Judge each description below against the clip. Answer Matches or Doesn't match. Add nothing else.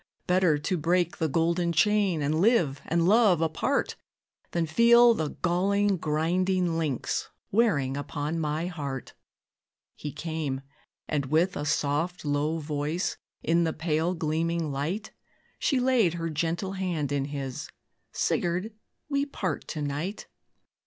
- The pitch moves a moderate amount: Matches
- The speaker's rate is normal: Doesn't match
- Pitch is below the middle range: Doesn't match